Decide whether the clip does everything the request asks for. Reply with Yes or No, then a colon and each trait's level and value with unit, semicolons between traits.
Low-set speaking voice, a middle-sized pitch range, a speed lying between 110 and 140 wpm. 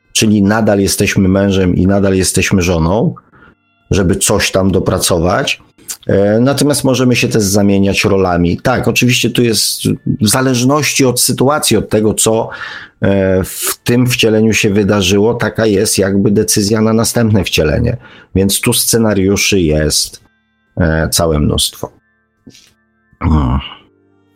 Yes: low, 105 Hz; average, 3.0 semitones; average, 120 wpm